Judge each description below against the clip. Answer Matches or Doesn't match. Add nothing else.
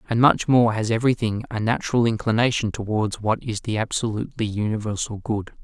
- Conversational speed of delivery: Matches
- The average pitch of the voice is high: Doesn't match